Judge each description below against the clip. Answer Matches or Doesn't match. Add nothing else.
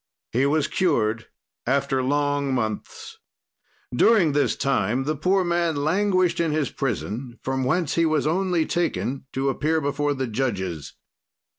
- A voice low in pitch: Doesn't match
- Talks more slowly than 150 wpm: Matches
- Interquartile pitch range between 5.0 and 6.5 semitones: Doesn't match